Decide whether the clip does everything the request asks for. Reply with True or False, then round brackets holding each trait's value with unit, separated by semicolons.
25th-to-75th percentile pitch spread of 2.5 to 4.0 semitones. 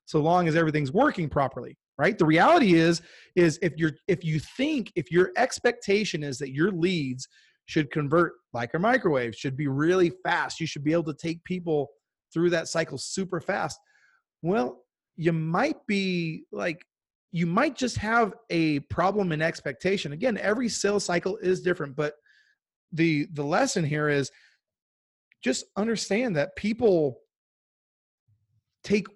False (4.5 semitones)